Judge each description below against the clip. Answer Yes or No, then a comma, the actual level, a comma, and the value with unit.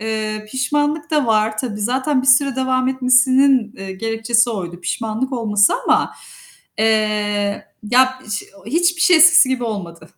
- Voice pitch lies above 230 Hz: Yes, high, 240 Hz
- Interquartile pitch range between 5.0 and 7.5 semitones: No, average, 3.6 semitones